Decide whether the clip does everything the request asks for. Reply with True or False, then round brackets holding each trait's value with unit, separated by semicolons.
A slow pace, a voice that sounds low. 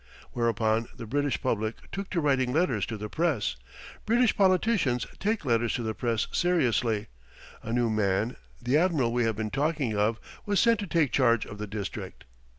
False (175 wpm; 120 Hz)